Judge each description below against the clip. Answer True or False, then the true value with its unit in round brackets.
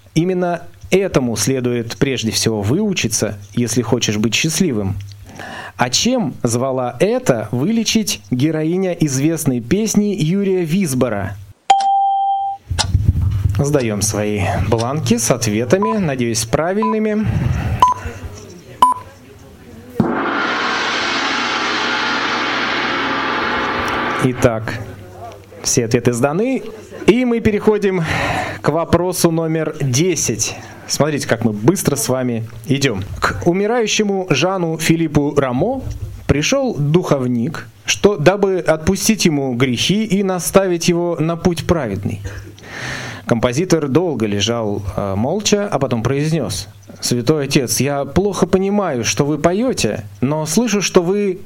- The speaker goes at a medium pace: False (95 wpm)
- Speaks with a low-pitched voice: False (145 Hz)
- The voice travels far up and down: True (8.4 semitones)